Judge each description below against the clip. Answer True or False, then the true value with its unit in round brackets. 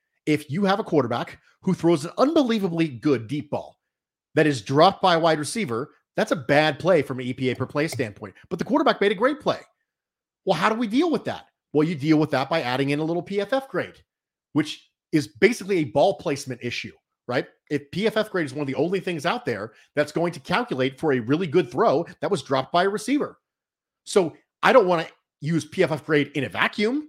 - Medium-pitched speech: True (160 Hz)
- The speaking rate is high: True (220 wpm)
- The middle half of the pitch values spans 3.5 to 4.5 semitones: False (5.2 semitones)